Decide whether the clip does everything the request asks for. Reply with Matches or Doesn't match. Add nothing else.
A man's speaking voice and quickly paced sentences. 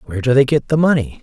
Matches